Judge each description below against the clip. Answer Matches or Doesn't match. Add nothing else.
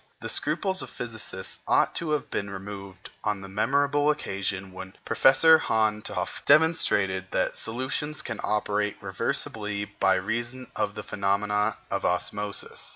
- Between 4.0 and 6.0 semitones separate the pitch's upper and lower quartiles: Matches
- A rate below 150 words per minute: Matches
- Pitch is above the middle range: Doesn't match